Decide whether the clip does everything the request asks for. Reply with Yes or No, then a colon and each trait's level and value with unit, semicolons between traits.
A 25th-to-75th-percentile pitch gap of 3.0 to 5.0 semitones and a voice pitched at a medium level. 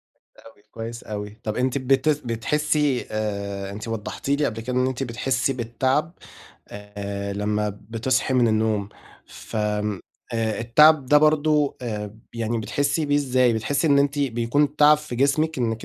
No: average, 4.7 semitones; low, 120 Hz